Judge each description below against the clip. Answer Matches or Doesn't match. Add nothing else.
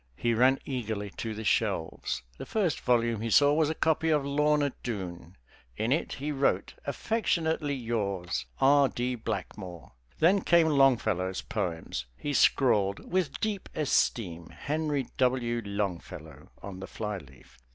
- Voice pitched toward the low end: Matches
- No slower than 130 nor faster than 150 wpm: Matches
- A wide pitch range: Matches